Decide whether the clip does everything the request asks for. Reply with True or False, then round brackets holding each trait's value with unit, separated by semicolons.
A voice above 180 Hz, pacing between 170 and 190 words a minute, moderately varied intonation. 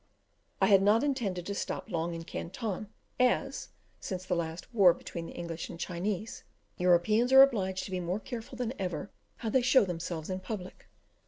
True (190 Hz; 180 wpm; 4.6 semitones)